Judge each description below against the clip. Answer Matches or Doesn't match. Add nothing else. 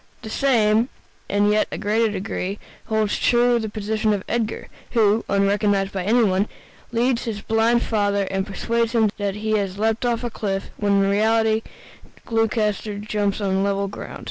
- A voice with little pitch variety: Matches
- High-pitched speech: Matches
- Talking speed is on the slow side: Doesn't match